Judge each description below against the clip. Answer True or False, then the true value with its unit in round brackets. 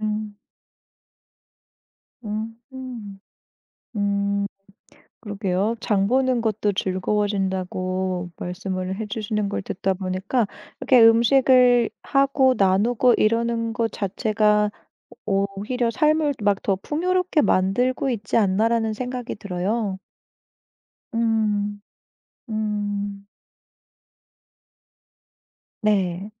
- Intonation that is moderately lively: True (3.0 semitones)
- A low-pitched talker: False (210 Hz)